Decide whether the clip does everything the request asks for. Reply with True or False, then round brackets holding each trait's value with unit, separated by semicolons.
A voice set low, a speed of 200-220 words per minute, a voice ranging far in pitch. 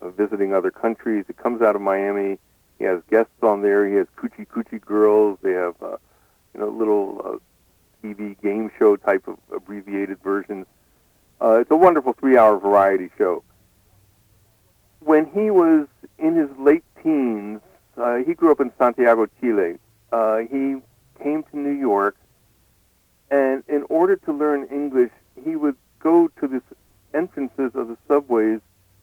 False (110 Hz; 155 wpm; 6.0 semitones)